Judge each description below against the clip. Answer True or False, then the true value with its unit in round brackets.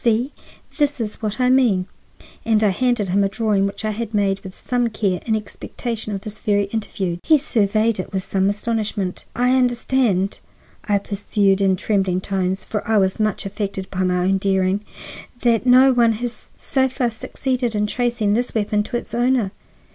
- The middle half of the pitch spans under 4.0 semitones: True (3.4 semitones)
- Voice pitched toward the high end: True (215 Hz)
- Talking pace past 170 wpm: True (185 wpm)